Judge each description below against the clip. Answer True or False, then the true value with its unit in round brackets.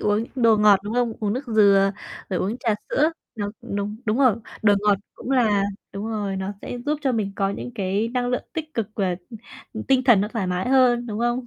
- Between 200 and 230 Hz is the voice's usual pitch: True (220 Hz)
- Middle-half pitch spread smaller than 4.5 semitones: True (3.4 semitones)